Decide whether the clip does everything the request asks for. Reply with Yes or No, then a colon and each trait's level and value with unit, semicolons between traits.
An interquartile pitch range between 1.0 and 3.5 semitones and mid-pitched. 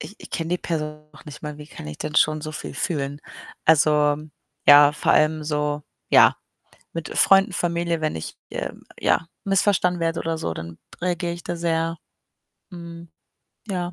Yes: narrow, 2.4 semitones; medium, 160 Hz